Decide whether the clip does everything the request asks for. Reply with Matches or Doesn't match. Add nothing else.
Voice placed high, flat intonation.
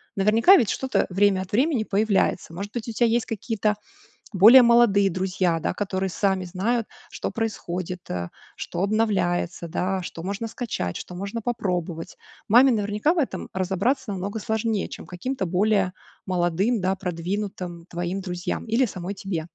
Doesn't match